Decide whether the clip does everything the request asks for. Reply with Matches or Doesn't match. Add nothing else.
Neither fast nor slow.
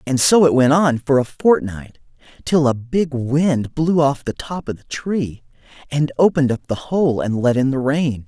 Doesn't match